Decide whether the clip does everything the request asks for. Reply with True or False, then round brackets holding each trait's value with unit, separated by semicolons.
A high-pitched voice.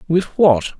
False (165 Hz)